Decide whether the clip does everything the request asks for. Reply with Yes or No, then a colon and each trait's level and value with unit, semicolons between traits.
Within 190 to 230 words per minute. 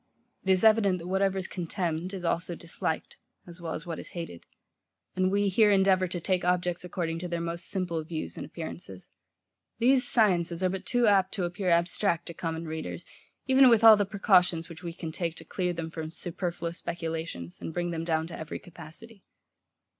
Yes: average, 195 wpm